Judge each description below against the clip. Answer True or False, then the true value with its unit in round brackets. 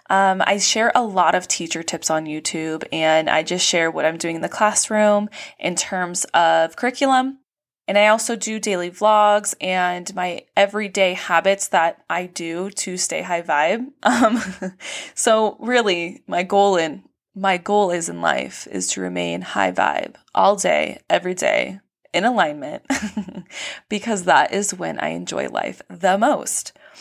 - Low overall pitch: False (190 Hz)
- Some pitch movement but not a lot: True (4.0 semitones)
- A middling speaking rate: True (160 wpm)